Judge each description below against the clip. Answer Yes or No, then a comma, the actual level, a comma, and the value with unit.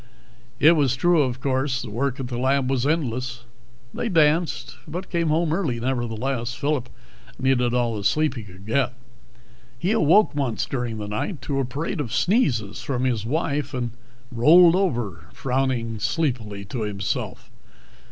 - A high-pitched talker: No, low, 130 Hz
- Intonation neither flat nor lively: Yes, average, 4.3 semitones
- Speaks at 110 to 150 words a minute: No, average, 160 wpm